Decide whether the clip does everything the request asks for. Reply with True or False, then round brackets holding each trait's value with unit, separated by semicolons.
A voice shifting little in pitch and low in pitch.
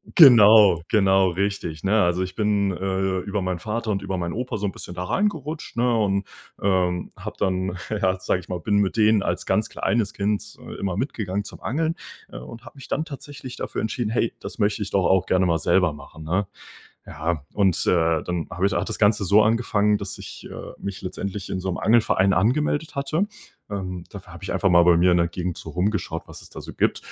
False (3.1 semitones; 100 Hz)